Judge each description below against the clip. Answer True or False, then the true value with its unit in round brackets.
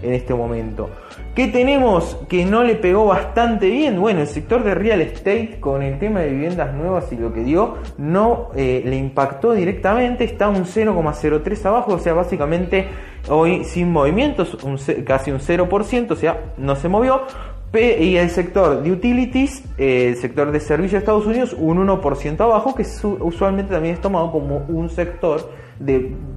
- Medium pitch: True (175 Hz)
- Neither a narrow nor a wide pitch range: False (6.7 semitones)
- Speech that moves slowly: False (170 wpm)